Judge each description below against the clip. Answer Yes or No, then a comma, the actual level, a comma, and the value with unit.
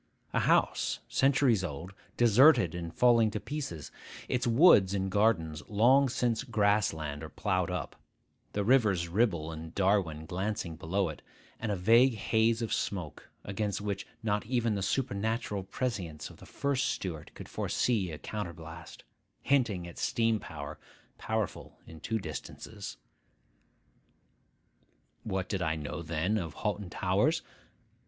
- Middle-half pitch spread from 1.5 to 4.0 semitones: No, average, 5.1 semitones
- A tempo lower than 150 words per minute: Yes, average, 140 wpm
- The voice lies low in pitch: Yes, low, 100 Hz